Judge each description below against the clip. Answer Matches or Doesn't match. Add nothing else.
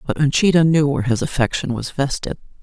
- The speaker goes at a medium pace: Matches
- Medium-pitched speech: Matches